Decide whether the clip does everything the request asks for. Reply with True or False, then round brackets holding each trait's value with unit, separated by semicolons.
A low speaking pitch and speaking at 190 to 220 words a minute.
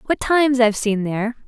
False (235 Hz; 205 wpm)